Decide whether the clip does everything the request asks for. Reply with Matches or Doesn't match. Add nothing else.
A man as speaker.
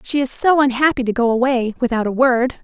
Doesn't match